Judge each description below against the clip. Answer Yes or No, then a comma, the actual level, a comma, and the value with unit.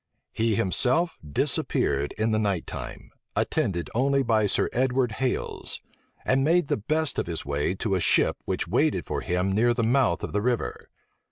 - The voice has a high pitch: No, low, 110 Hz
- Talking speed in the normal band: Yes, average, 175 wpm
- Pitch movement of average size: No, wide, 5.9 semitones